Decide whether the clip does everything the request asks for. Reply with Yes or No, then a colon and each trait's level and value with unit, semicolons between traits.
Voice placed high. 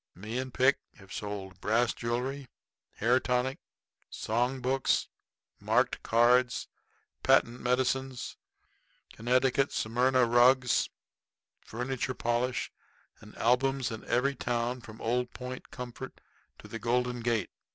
No: low, 125 Hz